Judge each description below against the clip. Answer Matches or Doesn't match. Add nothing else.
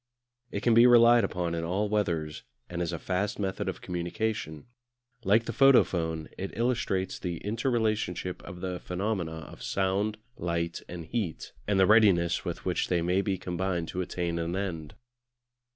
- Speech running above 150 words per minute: Matches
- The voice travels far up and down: Doesn't match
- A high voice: Doesn't match